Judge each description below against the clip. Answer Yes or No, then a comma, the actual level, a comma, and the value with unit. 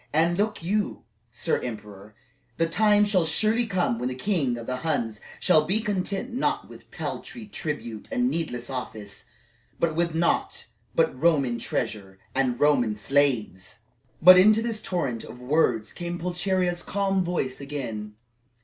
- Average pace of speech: Yes, average, 150 wpm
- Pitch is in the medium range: Yes, medium, 160 Hz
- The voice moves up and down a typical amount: No, wide, 7.5 semitones